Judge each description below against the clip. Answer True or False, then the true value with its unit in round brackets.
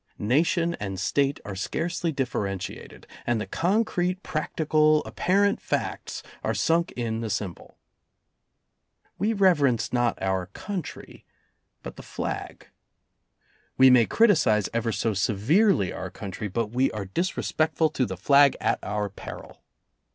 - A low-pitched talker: True (125 Hz)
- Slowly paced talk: True (130 wpm)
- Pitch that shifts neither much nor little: False (8.2 semitones)